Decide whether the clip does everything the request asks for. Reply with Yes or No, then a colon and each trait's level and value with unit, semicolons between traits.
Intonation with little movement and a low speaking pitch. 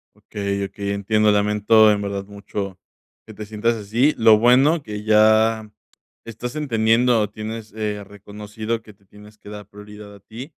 Yes: narrow, 1.5 semitones; low, 105 Hz